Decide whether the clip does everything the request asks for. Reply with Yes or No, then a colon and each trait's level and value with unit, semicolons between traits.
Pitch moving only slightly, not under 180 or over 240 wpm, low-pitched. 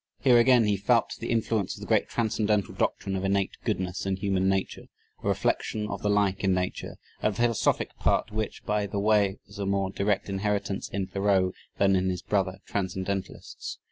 Yes: narrow, 1.7 semitones; average, 185 wpm; low, 100 Hz